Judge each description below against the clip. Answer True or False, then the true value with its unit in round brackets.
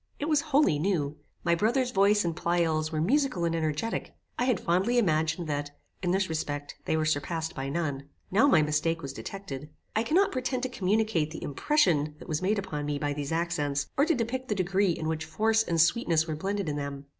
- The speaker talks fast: True (210 wpm)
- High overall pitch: False (170 Hz)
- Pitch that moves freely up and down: True (5.9 semitones)